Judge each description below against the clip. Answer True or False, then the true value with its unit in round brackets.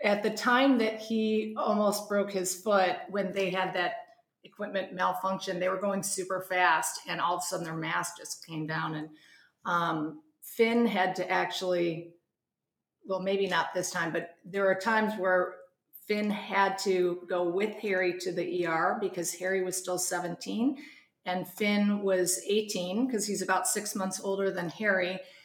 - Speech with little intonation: True (2.3 semitones)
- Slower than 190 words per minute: True (170 wpm)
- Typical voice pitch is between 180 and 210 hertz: True (190 Hz)